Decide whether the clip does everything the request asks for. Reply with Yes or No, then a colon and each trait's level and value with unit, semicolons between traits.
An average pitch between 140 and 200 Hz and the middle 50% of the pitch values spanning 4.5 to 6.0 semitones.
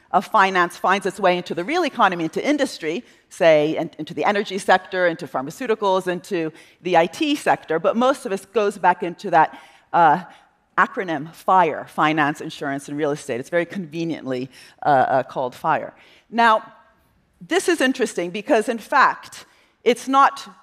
Yes: medium, 185 Hz; wide, 5.4 semitones